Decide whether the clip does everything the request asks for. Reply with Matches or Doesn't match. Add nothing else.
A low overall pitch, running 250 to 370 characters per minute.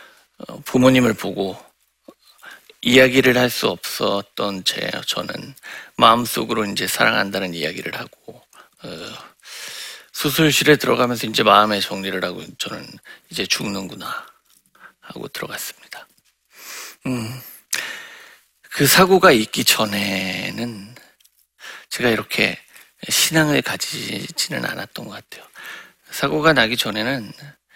Doesn't match